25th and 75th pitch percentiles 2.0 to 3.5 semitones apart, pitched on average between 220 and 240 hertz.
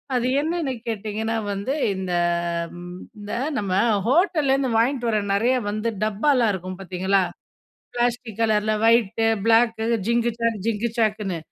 Yes: narrow, 2.6 semitones; high, 225 Hz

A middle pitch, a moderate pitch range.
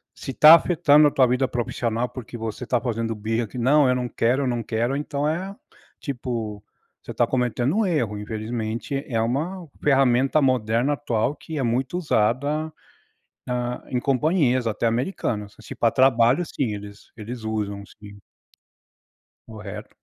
No: low, 125 Hz; average, 3.8 semitones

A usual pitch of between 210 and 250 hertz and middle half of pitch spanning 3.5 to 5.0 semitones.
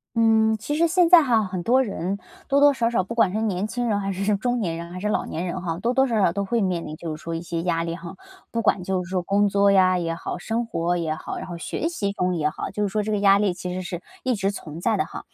No: high, 195 Hz; average, 4.2 semitones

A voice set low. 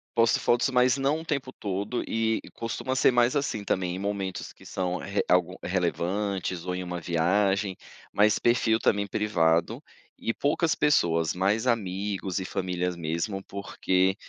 Yes: low, 100 Hz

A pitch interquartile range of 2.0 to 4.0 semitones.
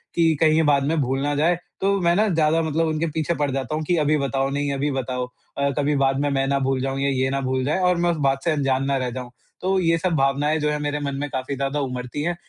Yes: average, 2.7 semitones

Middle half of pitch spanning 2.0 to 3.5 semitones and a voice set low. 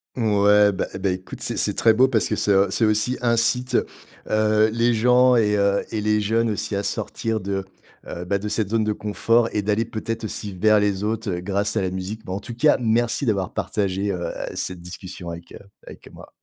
Yes: narrow, 2.4 semitones; low, 105 Hz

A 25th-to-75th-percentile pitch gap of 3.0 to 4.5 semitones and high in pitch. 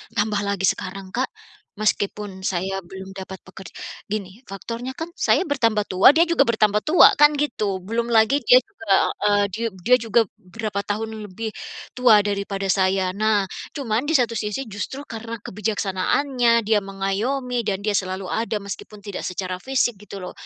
Yes: average, 3.3 semitones; high, 210 Hz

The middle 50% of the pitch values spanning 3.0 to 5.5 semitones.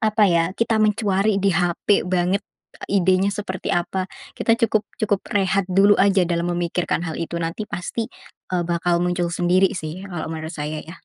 No: narrow, 2.6 semitones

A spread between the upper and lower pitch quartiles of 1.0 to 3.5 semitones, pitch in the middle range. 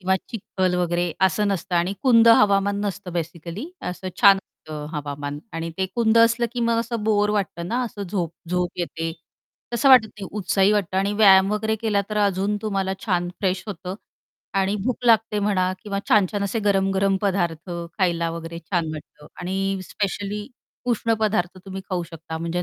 No: average, 3.0 semitones; high, 195 Hz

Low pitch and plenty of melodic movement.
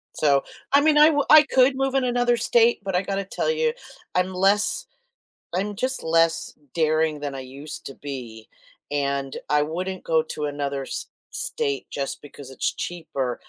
No: medium, 165 Hz; wide, 8.7 semitones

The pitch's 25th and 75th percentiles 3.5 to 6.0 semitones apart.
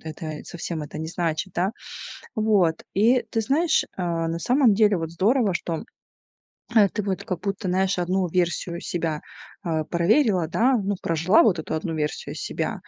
Yes: average, 4.1 semitones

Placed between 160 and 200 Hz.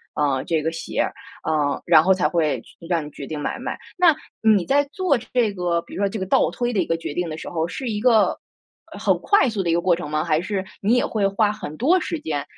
Yes: medium, 185 Hz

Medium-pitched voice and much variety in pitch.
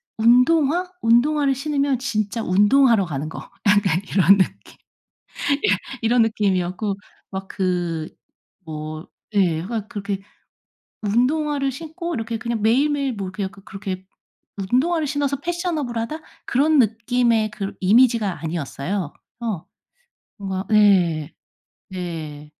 No: high, 215 Hz; wide, 6.1 semitones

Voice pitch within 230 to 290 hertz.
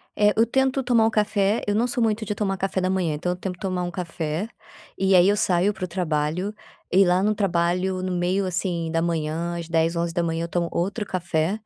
No: medium, 185 Hz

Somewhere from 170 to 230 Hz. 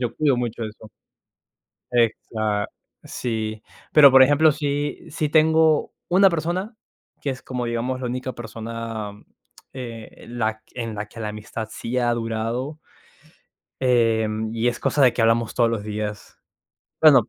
No: low, 120 Hz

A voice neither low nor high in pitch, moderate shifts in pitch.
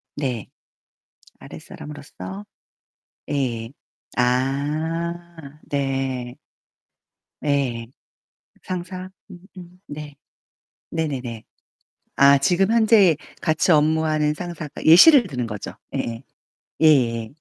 Yes: medium, 145 Hz; average, 4.5 semitones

